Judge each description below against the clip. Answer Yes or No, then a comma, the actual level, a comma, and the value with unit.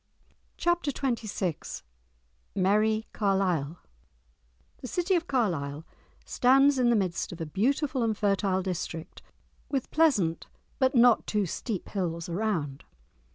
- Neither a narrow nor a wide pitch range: No, wide, 6.5 semitones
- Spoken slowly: Yes, slow, 115 wpm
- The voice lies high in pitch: Yes, high, 210 Hz